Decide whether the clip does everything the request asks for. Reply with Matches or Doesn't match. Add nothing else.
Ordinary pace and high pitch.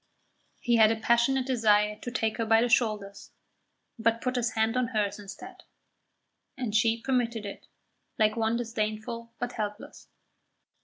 Matches